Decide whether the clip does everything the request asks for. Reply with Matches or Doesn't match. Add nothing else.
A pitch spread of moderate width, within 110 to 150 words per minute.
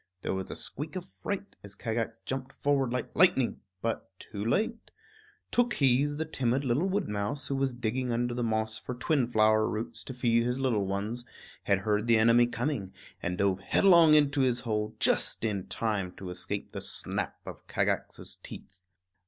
Doesn't match